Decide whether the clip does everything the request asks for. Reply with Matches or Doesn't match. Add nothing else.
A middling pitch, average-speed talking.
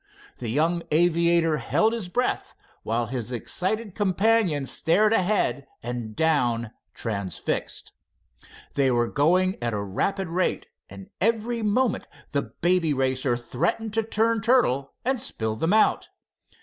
Doesn't match